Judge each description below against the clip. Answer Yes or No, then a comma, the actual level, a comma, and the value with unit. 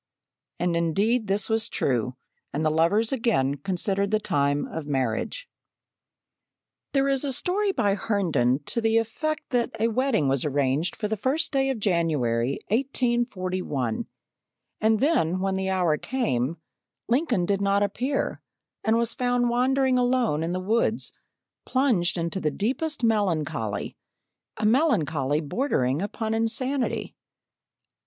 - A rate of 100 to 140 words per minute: Yes, slow, 135 wpm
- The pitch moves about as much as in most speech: No, wide, 7.7 semitones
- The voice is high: Yes, high, 205 Hz